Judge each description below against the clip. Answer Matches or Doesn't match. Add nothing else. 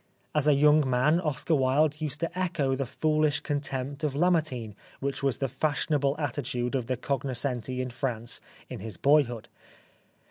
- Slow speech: Doesn't match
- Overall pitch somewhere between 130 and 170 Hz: Matches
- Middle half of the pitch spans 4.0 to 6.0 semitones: Doesn't match